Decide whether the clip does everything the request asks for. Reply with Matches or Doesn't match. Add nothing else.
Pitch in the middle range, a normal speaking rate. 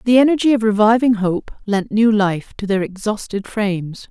Doesn't match